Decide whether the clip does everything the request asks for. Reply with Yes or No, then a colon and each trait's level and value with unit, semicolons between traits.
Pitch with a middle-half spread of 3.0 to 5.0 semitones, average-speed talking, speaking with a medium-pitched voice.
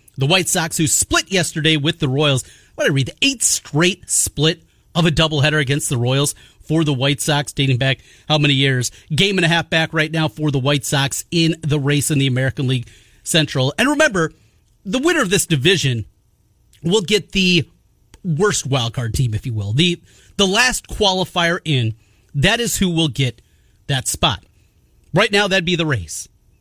No: wide, 5.5 semitones; average, 190 wpm; medium, 150 Hz